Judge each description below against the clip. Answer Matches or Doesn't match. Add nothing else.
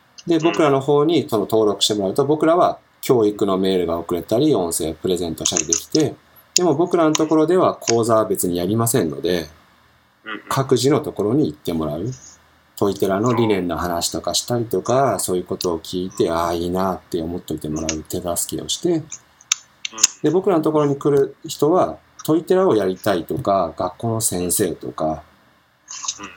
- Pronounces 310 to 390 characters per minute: Matches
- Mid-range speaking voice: Doesn't match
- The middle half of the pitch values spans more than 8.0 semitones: Matches